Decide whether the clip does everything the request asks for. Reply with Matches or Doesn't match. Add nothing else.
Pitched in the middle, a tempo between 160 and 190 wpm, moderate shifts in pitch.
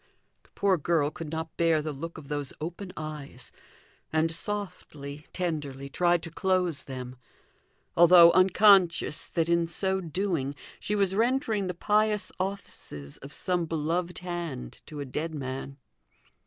Doesn't match